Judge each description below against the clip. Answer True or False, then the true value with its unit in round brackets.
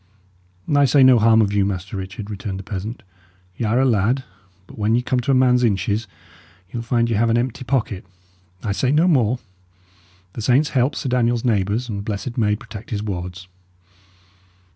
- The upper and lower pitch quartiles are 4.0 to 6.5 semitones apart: False (3.6 semitones)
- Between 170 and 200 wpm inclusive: True (195 wpm)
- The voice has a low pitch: True (115 Hz)